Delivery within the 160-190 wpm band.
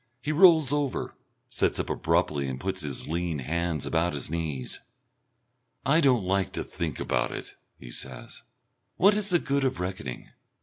Yes: average, 165 wpm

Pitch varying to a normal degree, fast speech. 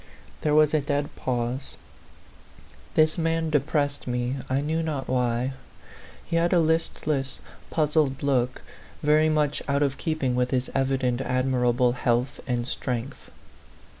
No: average, 3.4 semitones; average, 140 wpm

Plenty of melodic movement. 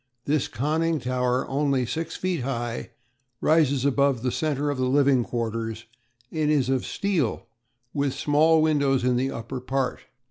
No: average, 3.1 semitones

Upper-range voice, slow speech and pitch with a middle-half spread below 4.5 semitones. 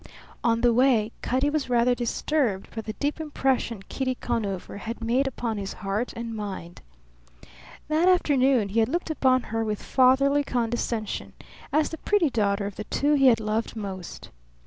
No: high, 240 Hz; average, 170 wpm; average, 4.1 semitones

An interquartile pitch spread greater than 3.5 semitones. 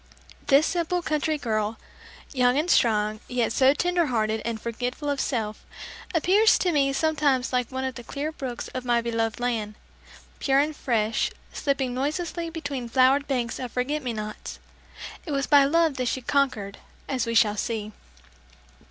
Yes: average, 4.0 semitones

